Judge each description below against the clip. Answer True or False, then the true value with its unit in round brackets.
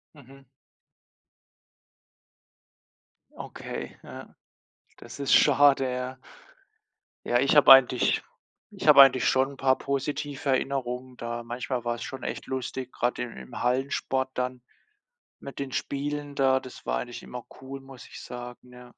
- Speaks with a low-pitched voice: True (130 Hz)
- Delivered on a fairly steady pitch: True (1.8 semitones)